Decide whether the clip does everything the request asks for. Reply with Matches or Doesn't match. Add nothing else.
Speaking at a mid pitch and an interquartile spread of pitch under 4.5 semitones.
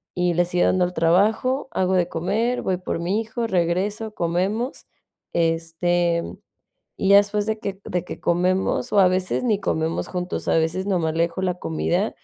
Matches